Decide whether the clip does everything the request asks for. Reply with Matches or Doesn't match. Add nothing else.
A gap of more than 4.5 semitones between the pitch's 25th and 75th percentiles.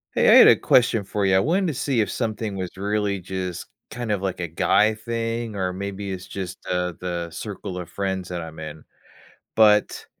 Doesn't match